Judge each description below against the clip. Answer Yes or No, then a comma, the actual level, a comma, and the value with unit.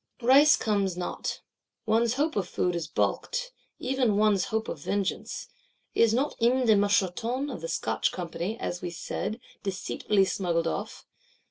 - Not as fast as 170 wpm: Yes, average, 150 wpm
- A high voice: Yes, high, 210 Hz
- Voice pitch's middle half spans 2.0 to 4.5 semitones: No, average, 5.1 semitones